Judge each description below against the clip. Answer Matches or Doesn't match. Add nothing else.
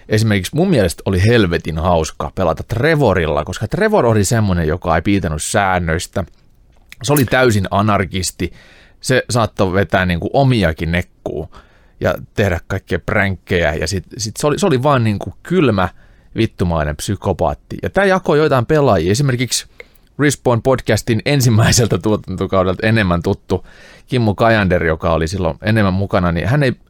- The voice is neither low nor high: Doesn't match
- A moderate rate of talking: Matches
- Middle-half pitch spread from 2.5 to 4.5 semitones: Doesn't match